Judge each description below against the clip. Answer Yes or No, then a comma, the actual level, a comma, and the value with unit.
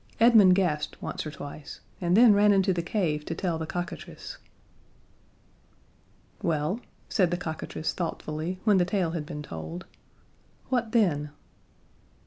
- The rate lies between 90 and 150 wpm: Yes, slow, 135 wpm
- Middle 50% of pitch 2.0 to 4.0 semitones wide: No, average, 4.4 semitones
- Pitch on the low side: No, medium, 175 Hz